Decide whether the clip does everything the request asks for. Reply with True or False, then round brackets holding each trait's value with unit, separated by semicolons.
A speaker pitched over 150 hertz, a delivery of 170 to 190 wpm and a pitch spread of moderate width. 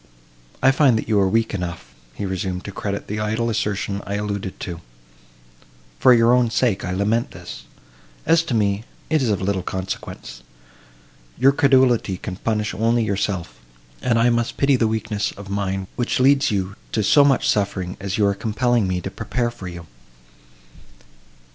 False (105 Hz; 175 wpm; 3.5 semitones)